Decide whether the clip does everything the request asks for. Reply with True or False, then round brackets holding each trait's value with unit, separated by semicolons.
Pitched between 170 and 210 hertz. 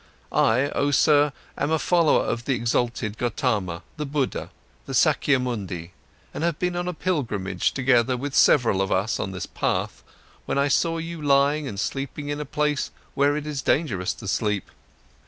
False (135 Hz)